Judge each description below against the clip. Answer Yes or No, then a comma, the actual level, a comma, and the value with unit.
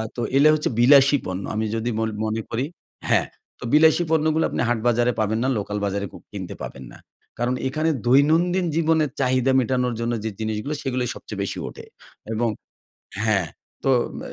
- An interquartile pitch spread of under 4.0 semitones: No, average, 5.3 semitones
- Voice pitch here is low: Yes, low, 125 Hz